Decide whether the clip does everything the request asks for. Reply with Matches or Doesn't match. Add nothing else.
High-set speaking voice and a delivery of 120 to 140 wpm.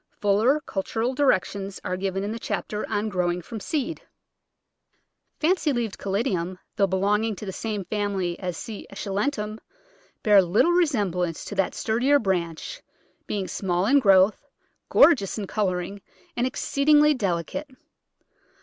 Matches